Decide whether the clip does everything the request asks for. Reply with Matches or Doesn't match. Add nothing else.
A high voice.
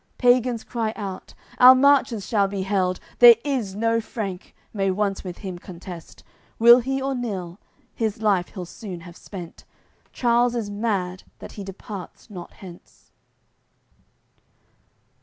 Matches